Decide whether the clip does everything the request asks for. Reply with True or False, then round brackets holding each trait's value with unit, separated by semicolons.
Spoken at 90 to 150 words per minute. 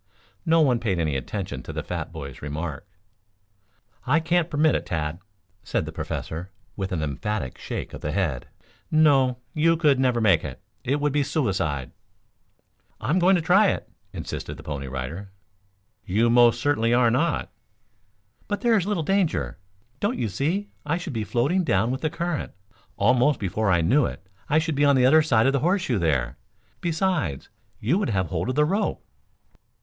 False (180 wpm)